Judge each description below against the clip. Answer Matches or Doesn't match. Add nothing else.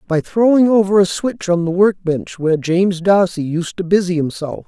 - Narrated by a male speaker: Matches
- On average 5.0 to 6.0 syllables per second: Matches